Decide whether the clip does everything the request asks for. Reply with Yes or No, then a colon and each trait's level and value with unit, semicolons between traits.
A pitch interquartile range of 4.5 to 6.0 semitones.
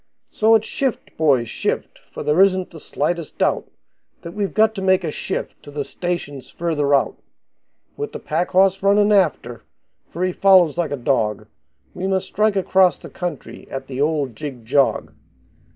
Yes: average, 5.2 semitones